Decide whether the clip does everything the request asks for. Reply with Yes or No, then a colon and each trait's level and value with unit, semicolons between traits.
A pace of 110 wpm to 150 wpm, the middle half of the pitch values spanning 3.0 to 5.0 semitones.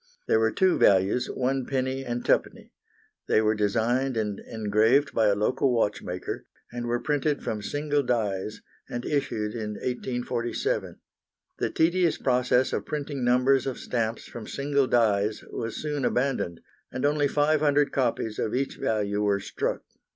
Yes: average, 145 wpm; average, 4.2 semitones